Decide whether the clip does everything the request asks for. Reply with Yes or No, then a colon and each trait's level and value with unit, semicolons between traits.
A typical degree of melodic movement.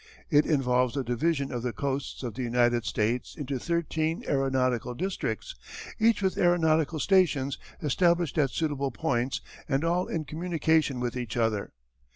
Yes: average, 4.8 semitones